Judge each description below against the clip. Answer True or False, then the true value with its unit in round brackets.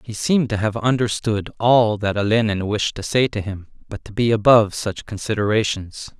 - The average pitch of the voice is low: True (110 Hz)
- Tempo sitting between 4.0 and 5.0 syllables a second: False (5.2 syllables/s)